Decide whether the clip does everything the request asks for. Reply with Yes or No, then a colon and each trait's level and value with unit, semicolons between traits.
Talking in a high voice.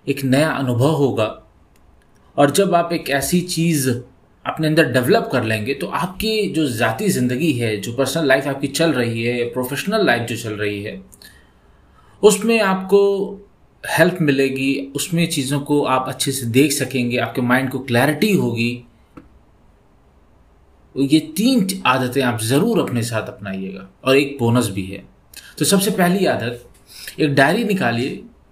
No: low, 135 Hz